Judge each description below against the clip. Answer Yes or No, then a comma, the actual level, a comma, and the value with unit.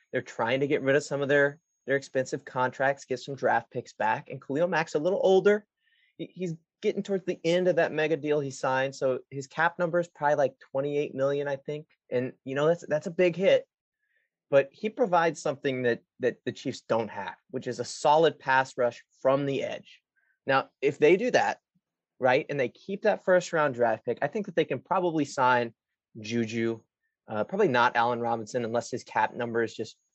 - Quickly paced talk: Yes, fast, 210 wpm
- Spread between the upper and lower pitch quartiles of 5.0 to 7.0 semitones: Yes, wide, 5.4 semitones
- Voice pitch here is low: No, medium, 145 Hz